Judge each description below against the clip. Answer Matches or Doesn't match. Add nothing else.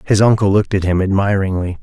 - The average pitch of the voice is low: Matches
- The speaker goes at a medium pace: Matches